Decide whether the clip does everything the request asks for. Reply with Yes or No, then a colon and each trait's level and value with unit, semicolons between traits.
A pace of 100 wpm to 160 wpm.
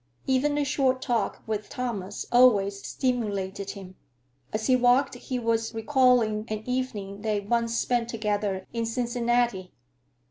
Yes: slow, 135 wpm